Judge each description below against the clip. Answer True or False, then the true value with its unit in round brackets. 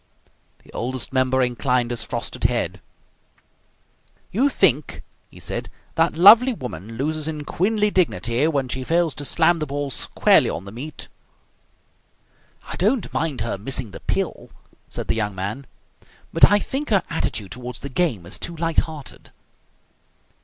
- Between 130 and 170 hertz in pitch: True (140 Hz)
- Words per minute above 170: False (155 wpm)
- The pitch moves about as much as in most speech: False (5.7 semitones)